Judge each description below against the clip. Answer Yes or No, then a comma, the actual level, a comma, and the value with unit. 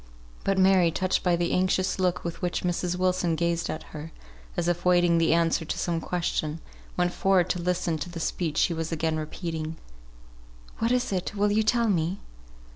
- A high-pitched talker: No, medium, 175 Hz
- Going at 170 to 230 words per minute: Yes, average, 190 wpm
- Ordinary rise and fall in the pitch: No, narrow, 2.0 semitones